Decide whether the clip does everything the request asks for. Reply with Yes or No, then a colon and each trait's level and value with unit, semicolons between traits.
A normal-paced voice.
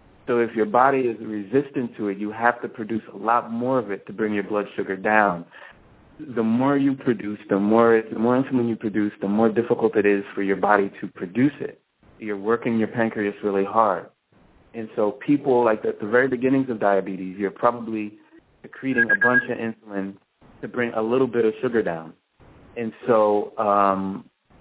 Yes: average, 195 wpm